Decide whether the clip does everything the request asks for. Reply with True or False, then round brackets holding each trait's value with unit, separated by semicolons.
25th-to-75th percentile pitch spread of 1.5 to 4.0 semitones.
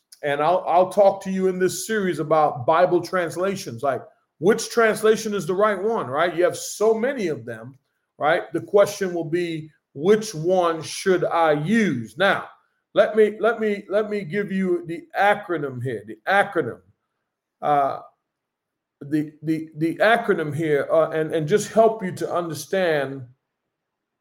False (4.6 semitones)